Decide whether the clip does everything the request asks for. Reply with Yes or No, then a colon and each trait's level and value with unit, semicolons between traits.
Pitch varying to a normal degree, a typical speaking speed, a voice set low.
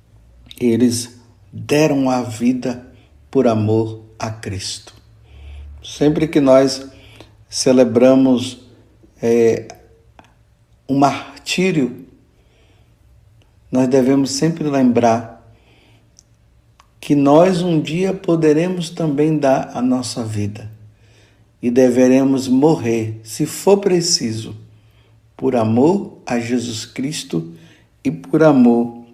No: average, 3.8 semitones; slow, 90 wpm; low, 120 Hz